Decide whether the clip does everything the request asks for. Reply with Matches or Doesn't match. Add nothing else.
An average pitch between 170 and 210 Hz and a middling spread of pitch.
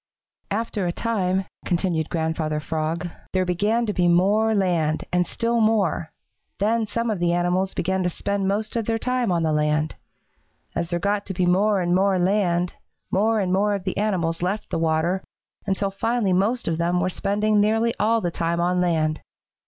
Matches